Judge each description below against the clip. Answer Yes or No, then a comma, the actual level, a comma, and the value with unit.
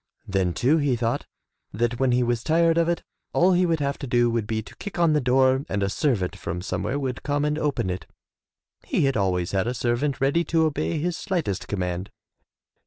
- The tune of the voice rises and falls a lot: Yes, wide, 6.5 semitones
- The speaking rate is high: Yes, fast, 220 wpm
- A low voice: Yes, low, 130 Hz